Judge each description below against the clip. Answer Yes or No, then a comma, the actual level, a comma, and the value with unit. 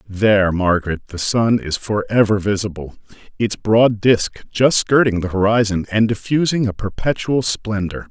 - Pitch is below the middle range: Yes, low, 105 Hz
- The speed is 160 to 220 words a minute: No, average, 140 wpm